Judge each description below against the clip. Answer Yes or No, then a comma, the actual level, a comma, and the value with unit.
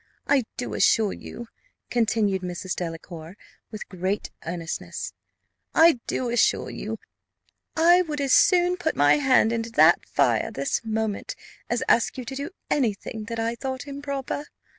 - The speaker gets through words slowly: No, average, 150 wpm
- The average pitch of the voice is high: Yes, high, 235 Hz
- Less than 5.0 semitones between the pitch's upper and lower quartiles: No, wide, 5.4 semitones